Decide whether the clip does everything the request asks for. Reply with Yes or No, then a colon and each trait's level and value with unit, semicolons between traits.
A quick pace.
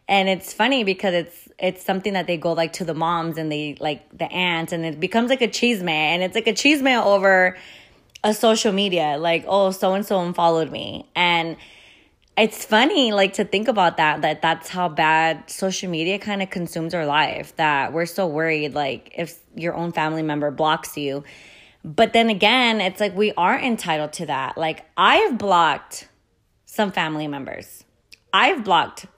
No: average, 185 wpm